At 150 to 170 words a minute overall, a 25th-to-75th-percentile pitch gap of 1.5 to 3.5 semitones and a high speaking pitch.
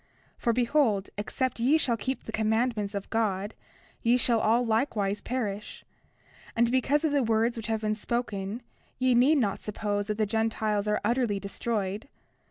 Yes: average, 165 wpm; average, 2.7 semitones; high, 225 Hz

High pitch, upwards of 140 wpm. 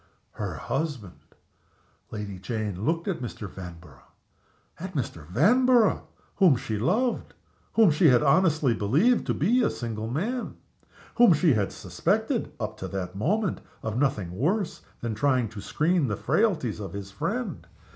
No: low, 135 Hz; average, 150 wpm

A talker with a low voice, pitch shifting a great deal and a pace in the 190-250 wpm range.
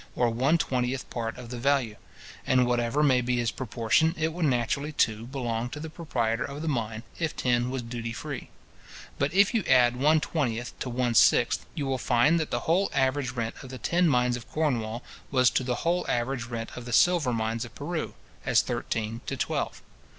No: low, 125 Hz; average, 3.7 semitones; average, 200 wpm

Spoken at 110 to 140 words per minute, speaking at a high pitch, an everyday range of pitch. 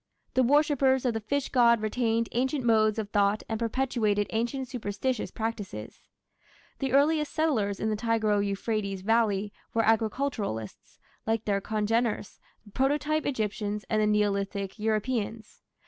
Yes: slow, 135 wpm; high, 225 Hz; average, 3.4 semitones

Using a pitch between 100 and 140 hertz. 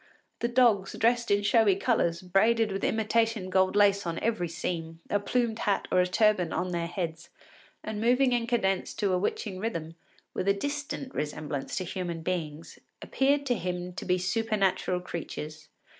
No: high, 195 Hz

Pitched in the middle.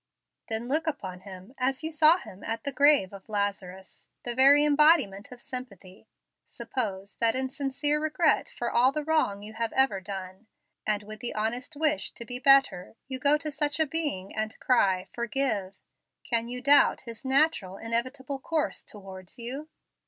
No: high, 245 Hz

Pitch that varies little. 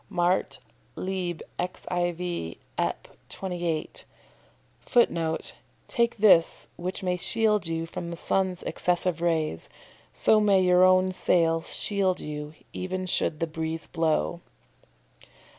Yes: narrow, 2.2 semitones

